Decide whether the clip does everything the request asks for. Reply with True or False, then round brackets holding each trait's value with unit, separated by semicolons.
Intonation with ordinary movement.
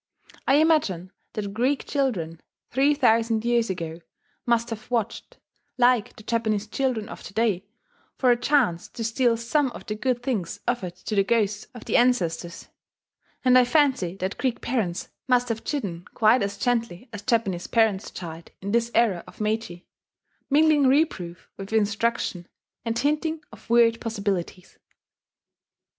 True (4.0 semitones)